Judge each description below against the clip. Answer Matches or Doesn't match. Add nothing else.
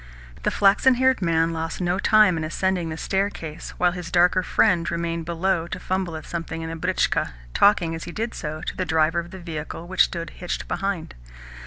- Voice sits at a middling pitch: Matches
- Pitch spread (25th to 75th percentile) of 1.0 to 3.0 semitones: Matches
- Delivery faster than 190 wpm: Matches